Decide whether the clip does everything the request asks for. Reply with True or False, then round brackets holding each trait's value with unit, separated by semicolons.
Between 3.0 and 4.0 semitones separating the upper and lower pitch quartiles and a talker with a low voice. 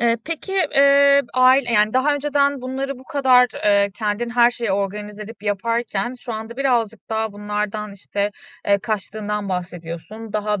False (3.7 semitones; 220 Hz)